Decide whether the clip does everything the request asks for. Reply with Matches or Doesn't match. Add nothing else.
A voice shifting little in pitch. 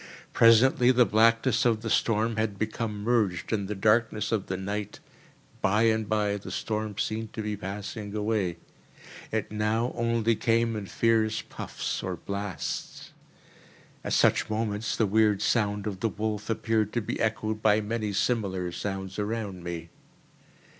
Matches